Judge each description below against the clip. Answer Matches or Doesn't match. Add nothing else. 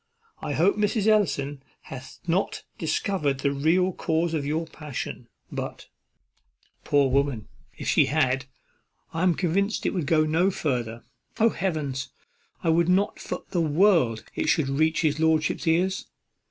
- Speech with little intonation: Doesn't match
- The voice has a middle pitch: Matches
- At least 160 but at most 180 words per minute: Doesn't match